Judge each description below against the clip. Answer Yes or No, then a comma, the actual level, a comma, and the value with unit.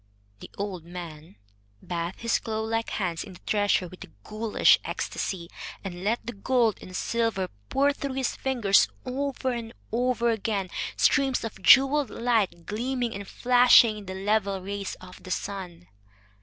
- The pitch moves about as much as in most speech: Yes, average, 4.4 semitones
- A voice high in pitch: Yes, high, 215 Hz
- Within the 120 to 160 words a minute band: Yes, average, 155 wpm